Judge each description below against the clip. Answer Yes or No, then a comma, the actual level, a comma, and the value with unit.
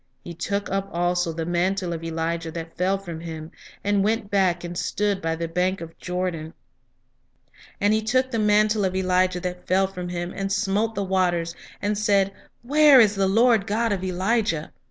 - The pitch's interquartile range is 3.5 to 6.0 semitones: No, average, 3.0 semitones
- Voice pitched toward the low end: No, high, 190 Hz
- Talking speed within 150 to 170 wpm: No, average, 185 wpm